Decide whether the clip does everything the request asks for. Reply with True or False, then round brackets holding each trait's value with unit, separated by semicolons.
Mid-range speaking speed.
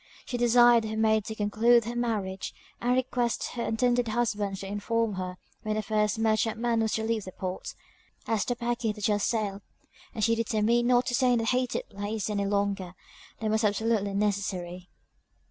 True (180 wpm)